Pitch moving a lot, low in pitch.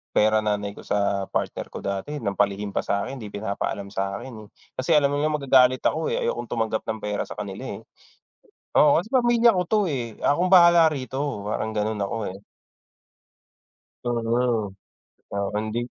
Yes: wide, 5.8 semitones; low, 115 Hz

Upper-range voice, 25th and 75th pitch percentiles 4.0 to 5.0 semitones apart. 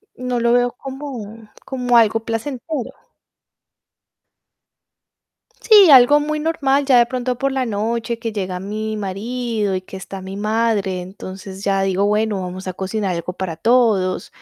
Yes: high, 225 Hz; average, 4.4 semitones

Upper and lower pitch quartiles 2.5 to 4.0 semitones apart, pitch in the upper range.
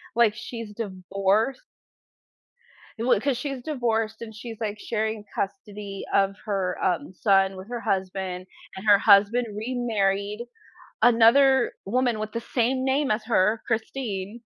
Yes: average, 3.3 semitones; high, 220 Hz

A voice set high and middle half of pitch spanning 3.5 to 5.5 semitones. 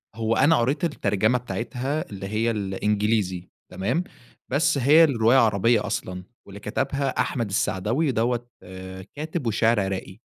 No: low, 115 Hz; average, 4.7 semitones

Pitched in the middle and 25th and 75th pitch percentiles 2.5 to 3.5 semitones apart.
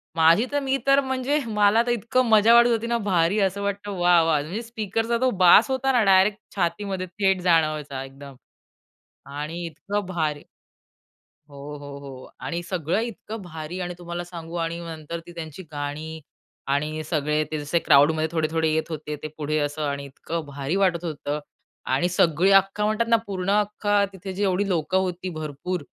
No: medium, 175 Hz; average, 4.8 semitones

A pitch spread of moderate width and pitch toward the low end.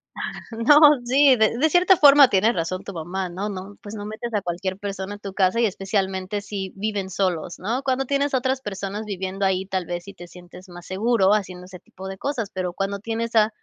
No: average, 3.5 semitones; high, 200 Hz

